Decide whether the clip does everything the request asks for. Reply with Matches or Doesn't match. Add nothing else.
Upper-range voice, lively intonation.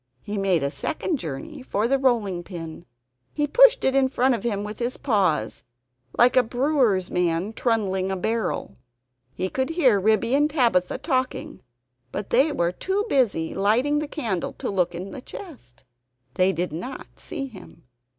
Matches